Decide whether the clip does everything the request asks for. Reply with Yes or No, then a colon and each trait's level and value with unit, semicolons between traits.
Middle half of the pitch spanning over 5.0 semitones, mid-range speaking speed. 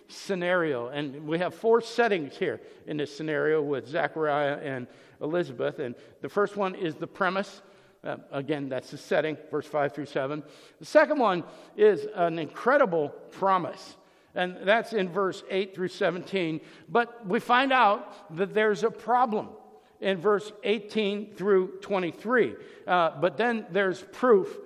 Yes: wide, 5.4 semitones; average, 150 wpm